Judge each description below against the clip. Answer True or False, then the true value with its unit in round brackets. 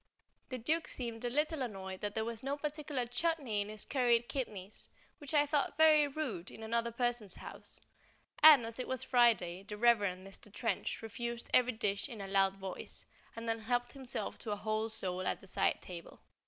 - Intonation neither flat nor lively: True (4.0 semitones)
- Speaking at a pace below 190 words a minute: False (195 wpm)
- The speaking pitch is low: False (235 Hz)